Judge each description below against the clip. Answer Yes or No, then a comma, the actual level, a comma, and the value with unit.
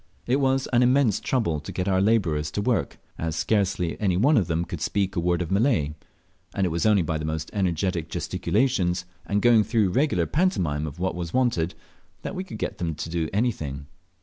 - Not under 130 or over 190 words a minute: No, average, 200 wpm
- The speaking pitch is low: Yes, very low, 95 Hz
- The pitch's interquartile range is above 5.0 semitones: Yes, wide, 5.6 semitones